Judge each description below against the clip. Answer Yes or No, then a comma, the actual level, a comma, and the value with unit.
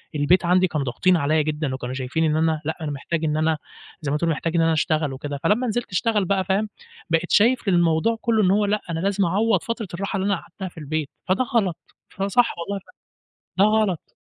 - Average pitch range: Yes, average, 4.3 semitones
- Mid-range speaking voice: Yes, medium, 175 Hz